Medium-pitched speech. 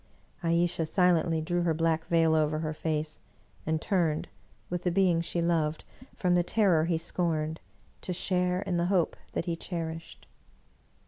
Yes: medium, 170 Hz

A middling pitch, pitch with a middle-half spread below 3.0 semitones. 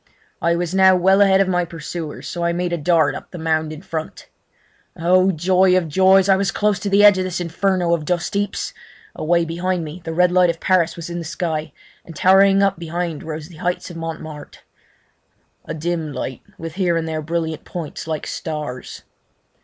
Yes: medium, 170 Hz; narrow, 2.4 semitones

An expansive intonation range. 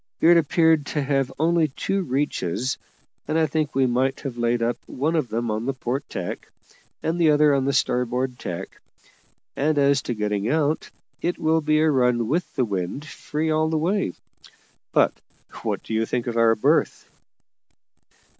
No: average, 4.6 semitones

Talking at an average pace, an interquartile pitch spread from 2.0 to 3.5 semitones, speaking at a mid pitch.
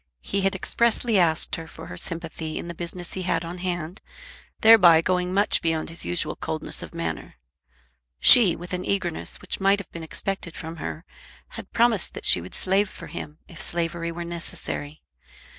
Yes: average, 180 wpm; average, 2.7 semitones; medium, 175 Hz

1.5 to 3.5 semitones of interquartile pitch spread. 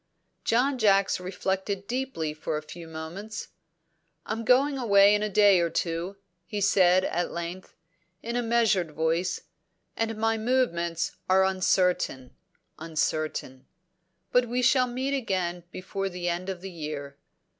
No: average, 4.8 semitones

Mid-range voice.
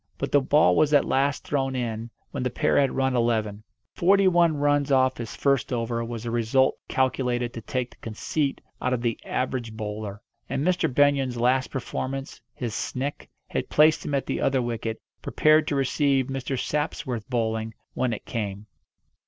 No: low, 130 Hz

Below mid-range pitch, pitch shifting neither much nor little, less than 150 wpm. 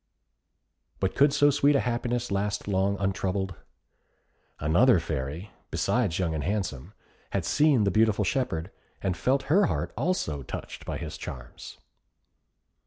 No: low, 100 Hz; wide, 6.4 semitones; slow, 135 wpm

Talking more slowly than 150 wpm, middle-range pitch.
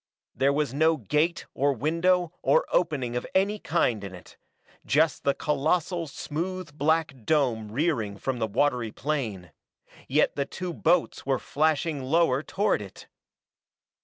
Yes: average, 140 wpm; medium, 150 Hz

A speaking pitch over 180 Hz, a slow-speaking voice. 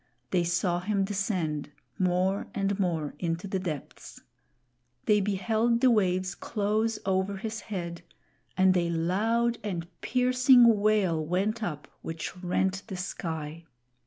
Yes: high, 190 Hz; slow, 130 wpm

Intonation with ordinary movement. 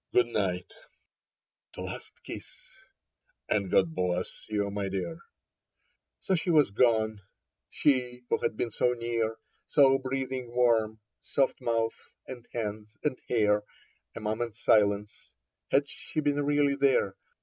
Yes: average, 4.1 semitones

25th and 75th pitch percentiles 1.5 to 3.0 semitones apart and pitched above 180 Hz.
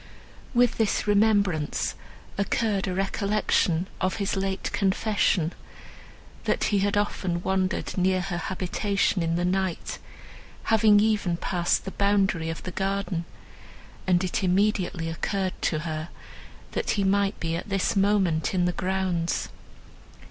Yes: narrow, 2.4 semitones; high, 190 Hz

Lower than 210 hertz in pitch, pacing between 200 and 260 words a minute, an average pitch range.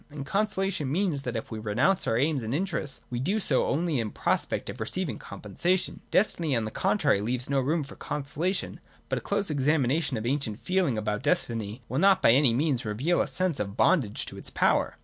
No: medium, 140 Hz; fast, 205 wpm; wide, 6.7 semitones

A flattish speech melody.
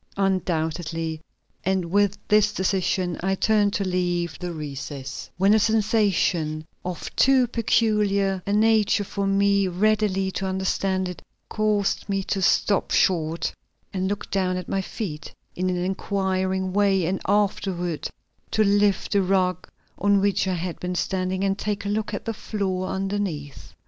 Yes: narrow, 2.0 semitones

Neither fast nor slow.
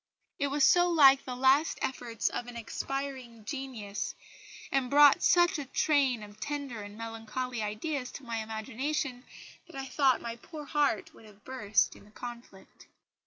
Yes: average, 165 wpm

